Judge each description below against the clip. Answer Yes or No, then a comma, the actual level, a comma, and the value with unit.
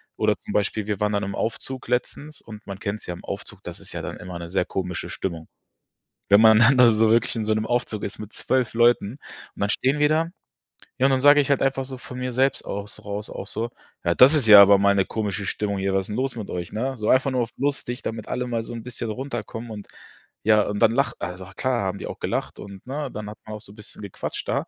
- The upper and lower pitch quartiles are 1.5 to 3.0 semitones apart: No, average, 4.0 semitones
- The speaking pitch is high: No, low, 110 Hz